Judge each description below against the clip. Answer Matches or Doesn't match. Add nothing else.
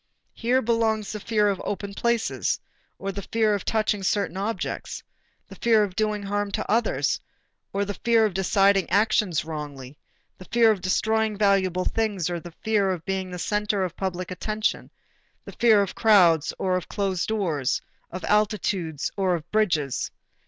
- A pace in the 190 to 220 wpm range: Doesn't match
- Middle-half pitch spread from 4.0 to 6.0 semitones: Doesn't match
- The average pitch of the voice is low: Doesn't match